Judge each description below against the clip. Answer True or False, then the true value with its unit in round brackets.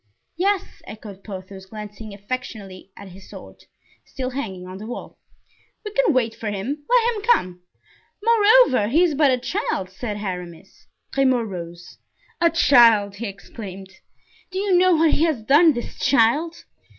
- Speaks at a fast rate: False (155 wpm)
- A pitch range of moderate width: False (8.7 semitones)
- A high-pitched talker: True (230 Hz)